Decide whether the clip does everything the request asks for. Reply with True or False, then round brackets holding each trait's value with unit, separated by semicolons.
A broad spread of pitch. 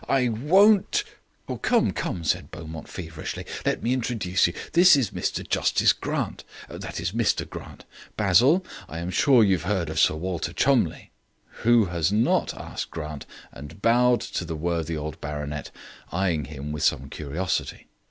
True (6.9 semitones)